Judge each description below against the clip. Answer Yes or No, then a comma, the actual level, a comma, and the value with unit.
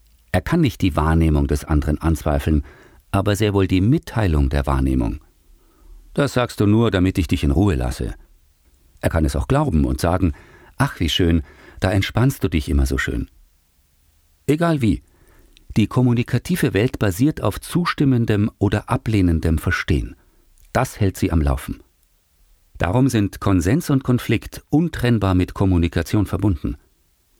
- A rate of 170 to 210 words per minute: No, average, 145 wpm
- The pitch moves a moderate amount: No, wide, 7.1 semitones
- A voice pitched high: No, very low, 95 Hz